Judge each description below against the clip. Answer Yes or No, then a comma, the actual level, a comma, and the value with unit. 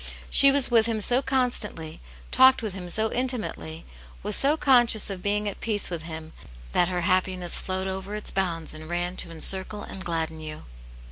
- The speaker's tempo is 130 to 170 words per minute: No, average, 185 wpm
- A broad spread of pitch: No, average, 4.6 semitones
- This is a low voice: No, high, 190 Hz